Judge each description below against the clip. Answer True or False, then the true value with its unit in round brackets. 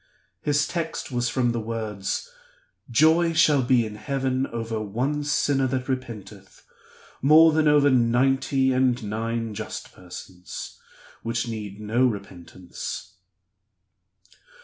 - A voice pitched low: True (120 Hz)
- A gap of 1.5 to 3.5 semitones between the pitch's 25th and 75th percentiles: False (3.9 semitones)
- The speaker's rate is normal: False (115 wpm)